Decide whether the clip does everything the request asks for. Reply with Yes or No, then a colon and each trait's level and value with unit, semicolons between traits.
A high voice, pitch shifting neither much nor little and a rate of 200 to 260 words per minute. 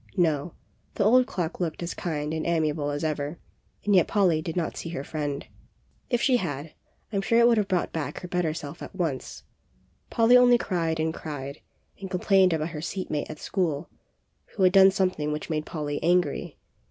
No: medium, 170 Hz; average, 3.9 semitones; fast, 205 wpm